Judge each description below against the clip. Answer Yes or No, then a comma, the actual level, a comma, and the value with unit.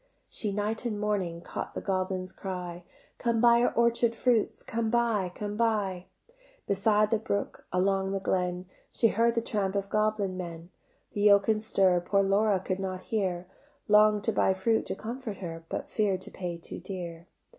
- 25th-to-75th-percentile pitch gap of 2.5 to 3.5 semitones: Yes, average, 2.9 semitones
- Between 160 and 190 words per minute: Yes, average, 175 wpm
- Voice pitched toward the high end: Yes, high, 200 Hz